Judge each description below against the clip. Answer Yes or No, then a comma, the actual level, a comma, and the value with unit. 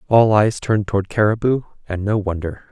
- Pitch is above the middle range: No, low, 105 Hz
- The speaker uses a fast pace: No, average, 175 wpm